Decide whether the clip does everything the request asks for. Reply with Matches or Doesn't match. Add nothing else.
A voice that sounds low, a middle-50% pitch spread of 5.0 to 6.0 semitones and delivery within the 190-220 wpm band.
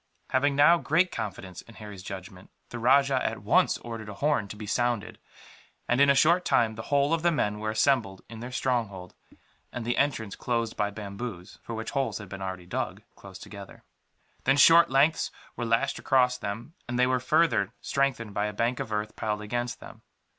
Doesn't match